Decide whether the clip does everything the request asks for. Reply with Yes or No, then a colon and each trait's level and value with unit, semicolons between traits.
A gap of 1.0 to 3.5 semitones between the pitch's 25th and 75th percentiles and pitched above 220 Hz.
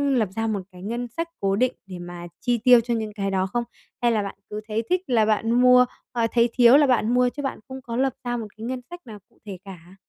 Yes: average, 3.1 semitones; high, 230 Hz